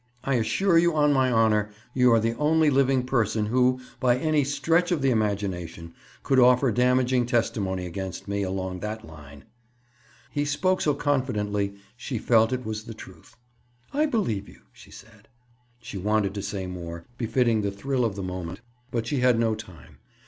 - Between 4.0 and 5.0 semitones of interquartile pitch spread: Yes, average, 4.7 semitones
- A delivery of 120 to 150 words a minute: No, average, 175 wpm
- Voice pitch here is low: Yes, low, 115 Hz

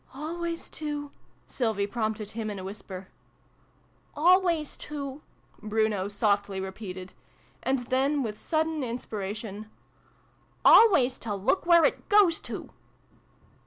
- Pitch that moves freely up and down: Yes, wide, 6.7 semitones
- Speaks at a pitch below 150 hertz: No, high, 235 Hz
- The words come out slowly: Yes, slow, 125 wpm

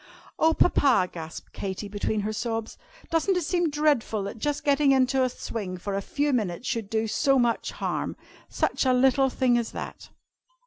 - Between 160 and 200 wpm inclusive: Yes, average, 180 wpm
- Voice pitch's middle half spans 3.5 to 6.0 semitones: Yes, average, 4.9 semitones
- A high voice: Yes, high, 245 Hz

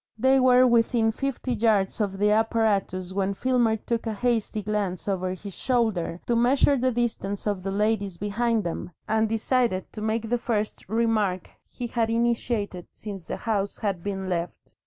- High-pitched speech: Yes, high, 220 Hz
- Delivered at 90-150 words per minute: No, average, 170 wpm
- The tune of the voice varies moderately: Yes, average, 3.2 semitones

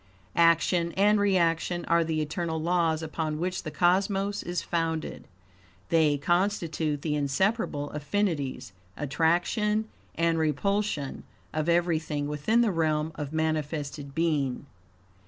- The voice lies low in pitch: No, medium, 165 Hz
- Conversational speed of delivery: No, slow, 115 wpm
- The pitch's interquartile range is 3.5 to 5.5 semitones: No, average, 2.9 semitones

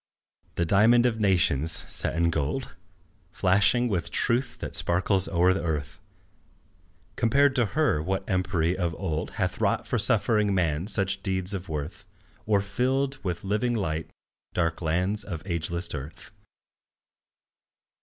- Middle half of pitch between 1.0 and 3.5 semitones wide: No, average, 4.1 semitones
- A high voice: No, very low, 95 Hz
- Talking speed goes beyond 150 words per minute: No, slow, 135 wpm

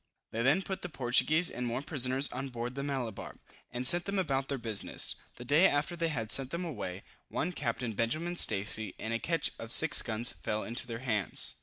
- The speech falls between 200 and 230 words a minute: Yes, fast, 205 wpm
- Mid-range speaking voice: No, low, 130 Hz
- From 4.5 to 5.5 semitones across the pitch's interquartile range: Yes, average, 5.2 semitones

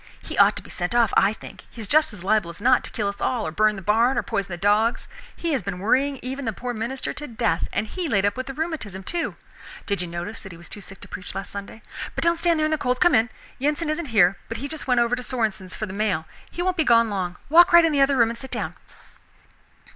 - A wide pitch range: Yes, wide, 5.7 semitones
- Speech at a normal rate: No, fast, 280 wpm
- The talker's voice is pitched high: Yes, high, 230 Hz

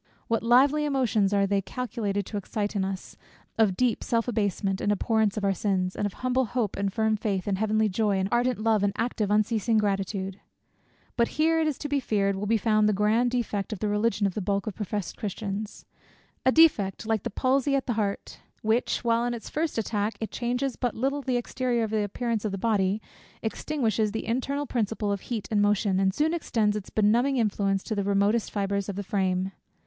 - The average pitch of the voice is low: No, high, 215 Hz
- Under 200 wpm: No, fast, 205 wpm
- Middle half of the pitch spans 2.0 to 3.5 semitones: Yes, average, 3.1 semitones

